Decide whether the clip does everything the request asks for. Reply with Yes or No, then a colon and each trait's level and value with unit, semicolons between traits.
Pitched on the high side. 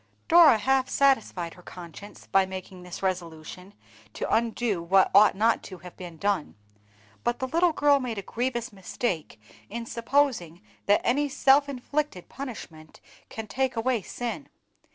Yes: high, 225 Hz